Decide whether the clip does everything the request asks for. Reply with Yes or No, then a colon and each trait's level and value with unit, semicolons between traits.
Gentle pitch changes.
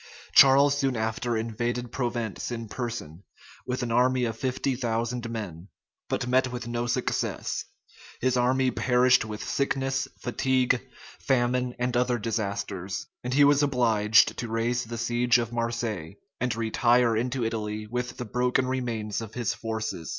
Yes: narrow, 1.9 semitones